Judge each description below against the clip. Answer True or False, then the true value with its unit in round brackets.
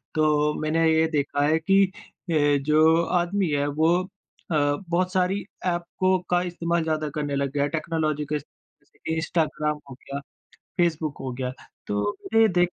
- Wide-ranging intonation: False (2.8 semitones)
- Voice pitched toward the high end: False (155 Hz)